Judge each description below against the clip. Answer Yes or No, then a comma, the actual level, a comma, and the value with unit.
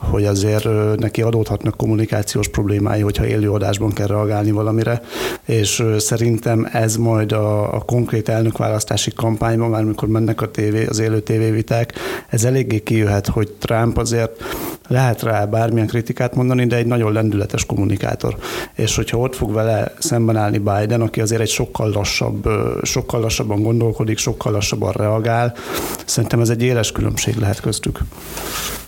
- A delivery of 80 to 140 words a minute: No, average, 150 wpm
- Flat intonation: Yes, narrow, 1.6 semitones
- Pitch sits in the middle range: No, low, 110 Hz